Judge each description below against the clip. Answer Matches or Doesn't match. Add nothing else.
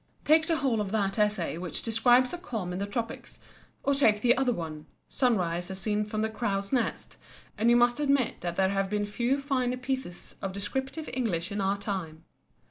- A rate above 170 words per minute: Matches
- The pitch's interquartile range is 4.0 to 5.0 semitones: Matches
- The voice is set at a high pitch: Matches